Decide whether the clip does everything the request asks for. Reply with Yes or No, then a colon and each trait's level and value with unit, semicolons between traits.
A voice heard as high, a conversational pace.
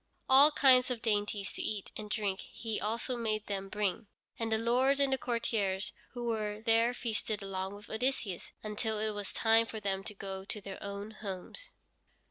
Yes: high, 215 Hz; average, 185 wpm